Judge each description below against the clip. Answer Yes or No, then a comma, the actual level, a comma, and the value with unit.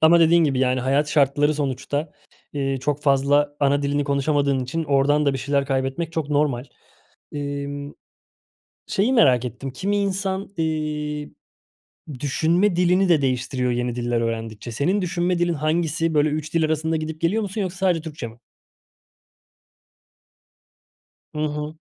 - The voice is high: No, medium, 150 Hz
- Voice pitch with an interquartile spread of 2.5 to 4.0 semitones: Yes, average, 3.2 semitones